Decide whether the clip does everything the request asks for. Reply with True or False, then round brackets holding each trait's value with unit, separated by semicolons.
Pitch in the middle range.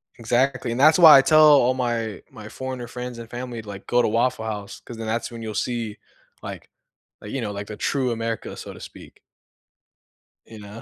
False (115 Hz)